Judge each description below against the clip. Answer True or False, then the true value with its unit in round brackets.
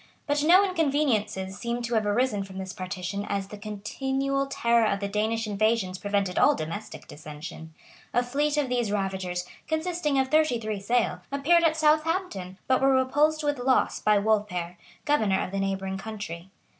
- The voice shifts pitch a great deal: True (6.0 semitones)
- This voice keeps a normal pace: True (170 wpm)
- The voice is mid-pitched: False (220 Hz)